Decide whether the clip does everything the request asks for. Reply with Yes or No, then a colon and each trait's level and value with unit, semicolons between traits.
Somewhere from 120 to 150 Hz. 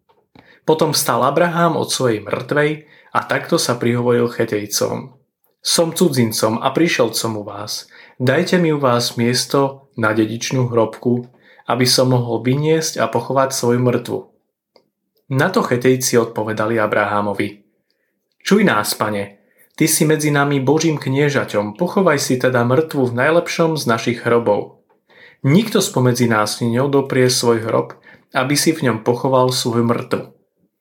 Yes: low, 125 Hz